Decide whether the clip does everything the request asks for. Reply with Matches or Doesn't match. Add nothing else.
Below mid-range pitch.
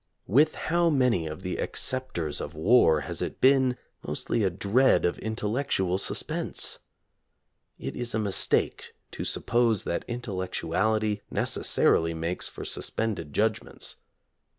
Matches